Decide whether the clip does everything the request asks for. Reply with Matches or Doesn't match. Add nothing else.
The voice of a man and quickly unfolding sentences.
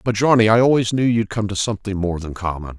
Matches